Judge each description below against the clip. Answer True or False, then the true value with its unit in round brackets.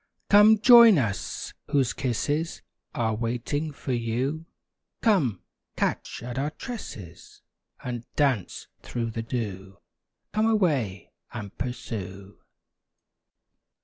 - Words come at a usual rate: False (100 wpm)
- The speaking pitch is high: False (125 Hz)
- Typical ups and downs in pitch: False (6.1 semitones)